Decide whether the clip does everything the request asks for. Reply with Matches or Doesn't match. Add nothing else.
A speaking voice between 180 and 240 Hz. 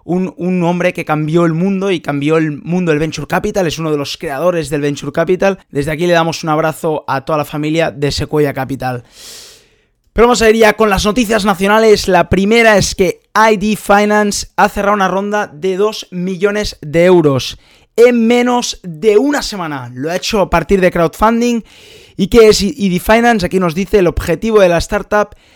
Matches